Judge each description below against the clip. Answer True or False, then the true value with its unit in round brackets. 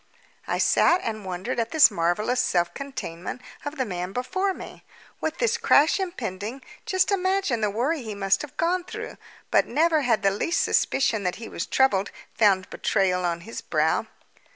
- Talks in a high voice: True (235 Hz)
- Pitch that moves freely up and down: True (8.2 semitones)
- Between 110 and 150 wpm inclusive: False (175 wpm)